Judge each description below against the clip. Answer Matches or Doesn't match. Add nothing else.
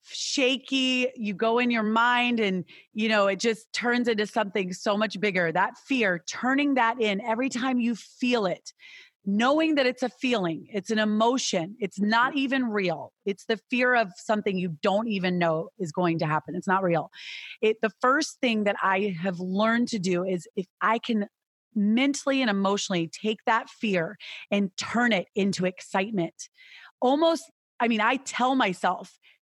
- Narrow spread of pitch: Doesn't match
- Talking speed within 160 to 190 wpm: Matches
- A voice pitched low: Doesn't match